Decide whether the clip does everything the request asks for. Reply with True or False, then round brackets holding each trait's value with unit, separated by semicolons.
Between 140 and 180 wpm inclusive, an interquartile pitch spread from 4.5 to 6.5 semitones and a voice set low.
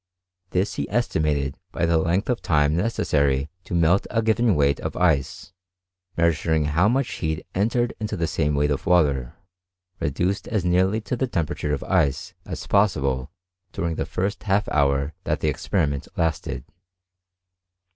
True (155 wpm; 5.4 semitones; 85 Hz)